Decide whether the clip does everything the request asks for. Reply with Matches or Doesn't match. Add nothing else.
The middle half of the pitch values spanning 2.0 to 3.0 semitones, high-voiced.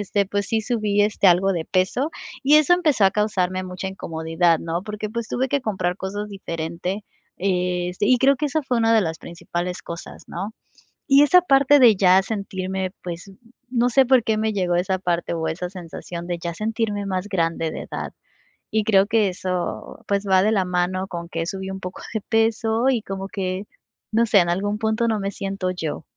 Doesn't match